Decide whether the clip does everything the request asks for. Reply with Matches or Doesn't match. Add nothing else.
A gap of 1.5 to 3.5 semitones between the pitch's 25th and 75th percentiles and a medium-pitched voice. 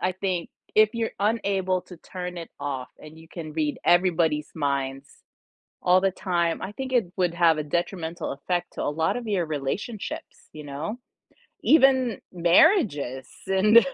Doesn't match